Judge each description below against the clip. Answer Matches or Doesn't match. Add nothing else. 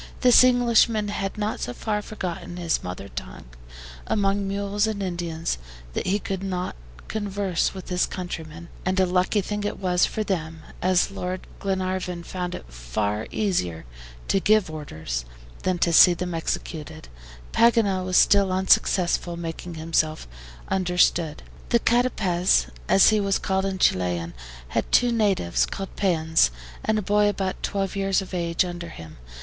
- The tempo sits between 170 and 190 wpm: Doesn't match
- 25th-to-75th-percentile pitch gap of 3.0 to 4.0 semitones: Matches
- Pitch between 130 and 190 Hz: Matches